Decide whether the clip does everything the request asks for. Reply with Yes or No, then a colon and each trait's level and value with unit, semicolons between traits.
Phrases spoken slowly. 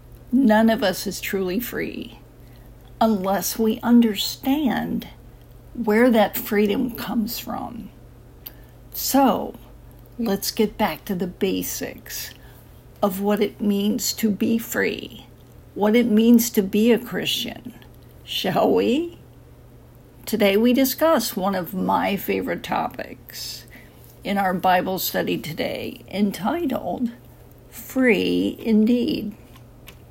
Yes: slow, 105 wpm